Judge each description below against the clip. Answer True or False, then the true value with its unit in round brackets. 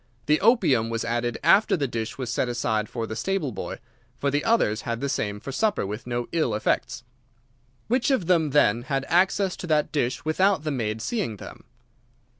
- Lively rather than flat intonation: True (6.9 semitones)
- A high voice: False (135 Hz)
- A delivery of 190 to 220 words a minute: True (195 wpm)